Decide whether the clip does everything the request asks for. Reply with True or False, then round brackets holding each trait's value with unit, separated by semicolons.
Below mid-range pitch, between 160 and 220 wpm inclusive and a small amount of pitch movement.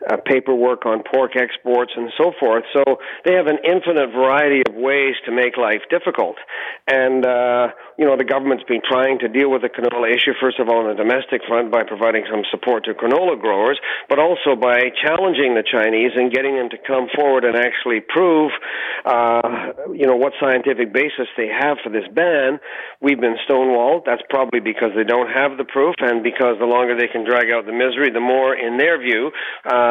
True (125 Hz; 205 wpm; 2.0 semitones)